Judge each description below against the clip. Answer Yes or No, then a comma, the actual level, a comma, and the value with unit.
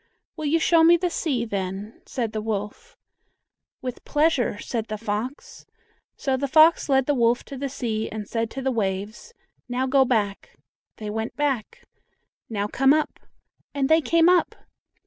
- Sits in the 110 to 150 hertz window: No, very high, 255 Hz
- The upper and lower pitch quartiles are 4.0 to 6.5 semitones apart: Yes, average, 5.3 semitones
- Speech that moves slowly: No, average, 165 wpm